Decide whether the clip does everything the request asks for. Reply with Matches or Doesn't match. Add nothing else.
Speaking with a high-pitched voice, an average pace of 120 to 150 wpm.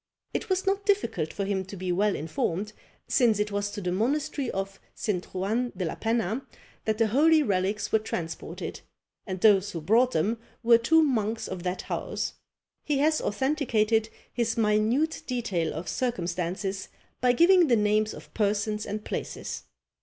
Doesn't match